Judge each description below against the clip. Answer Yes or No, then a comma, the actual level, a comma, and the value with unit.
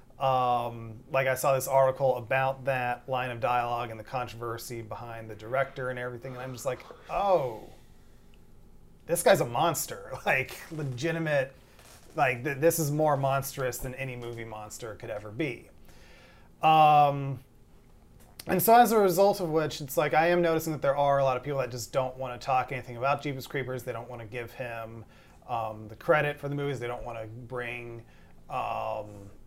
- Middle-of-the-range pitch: No, low, 130 Hz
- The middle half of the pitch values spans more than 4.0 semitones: No, average, 3.0 semitones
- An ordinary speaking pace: Yes, average, 185 wpm